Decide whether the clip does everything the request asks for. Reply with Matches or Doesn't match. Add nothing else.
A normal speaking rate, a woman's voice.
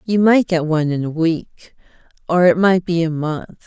Doesn't match